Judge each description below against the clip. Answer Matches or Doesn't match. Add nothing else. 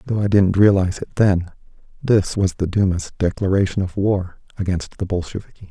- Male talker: Matches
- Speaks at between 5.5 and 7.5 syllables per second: Matches